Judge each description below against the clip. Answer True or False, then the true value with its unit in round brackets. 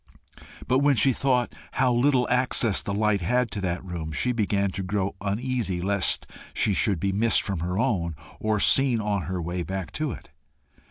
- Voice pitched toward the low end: True (100 Hz)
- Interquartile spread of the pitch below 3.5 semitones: False (4.9 semitones)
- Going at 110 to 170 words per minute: False (185 wpm)